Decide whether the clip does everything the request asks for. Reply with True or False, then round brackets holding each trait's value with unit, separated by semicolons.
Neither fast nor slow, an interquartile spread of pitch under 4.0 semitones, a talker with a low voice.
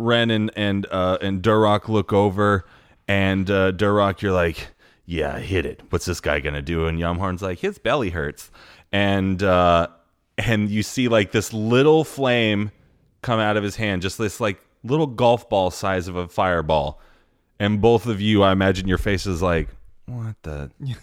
True (180 wpm; 3.1 semitones; 100 Hz)